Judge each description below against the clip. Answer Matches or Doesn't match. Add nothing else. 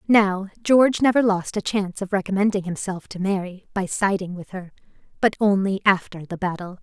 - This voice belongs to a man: Doesn't match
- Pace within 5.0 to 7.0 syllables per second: Matches